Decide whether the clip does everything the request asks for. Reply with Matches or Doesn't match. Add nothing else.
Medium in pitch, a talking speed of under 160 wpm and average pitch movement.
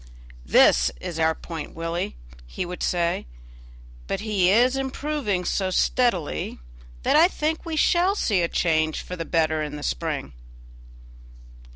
Doesn't match